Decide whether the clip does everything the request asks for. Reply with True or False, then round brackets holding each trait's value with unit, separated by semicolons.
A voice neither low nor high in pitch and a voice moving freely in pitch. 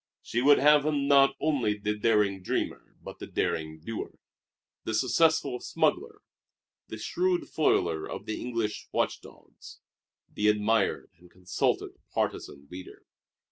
False (110 Hz; 5.9 semitones)